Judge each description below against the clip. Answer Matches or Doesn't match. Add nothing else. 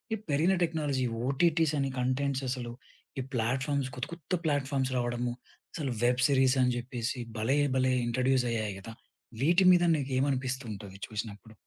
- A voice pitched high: Doesn't match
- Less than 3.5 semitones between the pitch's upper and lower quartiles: Matches